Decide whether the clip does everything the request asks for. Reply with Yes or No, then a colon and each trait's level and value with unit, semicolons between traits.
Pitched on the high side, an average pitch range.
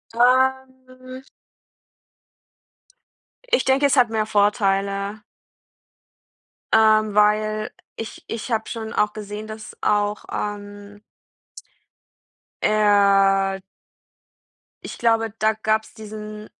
No: high, 215 Hz; narrow, 1.6 semitones